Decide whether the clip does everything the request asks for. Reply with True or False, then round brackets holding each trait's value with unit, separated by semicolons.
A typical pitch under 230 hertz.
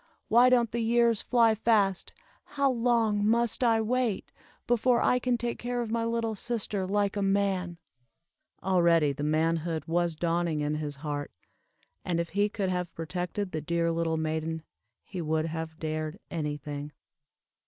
True (185 Hz)